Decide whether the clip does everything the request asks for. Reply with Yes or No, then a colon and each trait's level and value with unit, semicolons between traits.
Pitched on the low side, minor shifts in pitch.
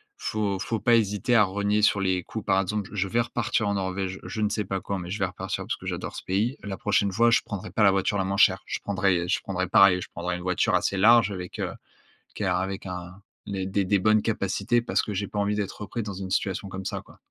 Yes: low, 100 Hz; narrow, 2.0 semitones